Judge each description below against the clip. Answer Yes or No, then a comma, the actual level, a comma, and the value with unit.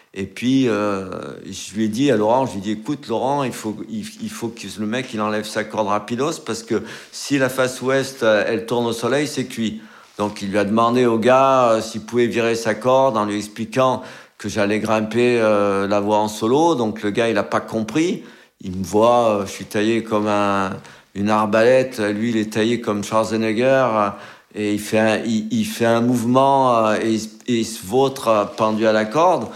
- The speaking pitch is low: Yes, low, 110 Hz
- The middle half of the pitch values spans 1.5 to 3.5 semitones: Yes, average, 2.8 semitones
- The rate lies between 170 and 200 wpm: No, average, 215 wpm